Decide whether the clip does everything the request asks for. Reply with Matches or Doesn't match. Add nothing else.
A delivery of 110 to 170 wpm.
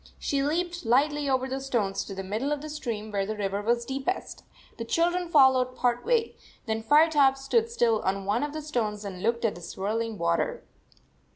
Doesn't match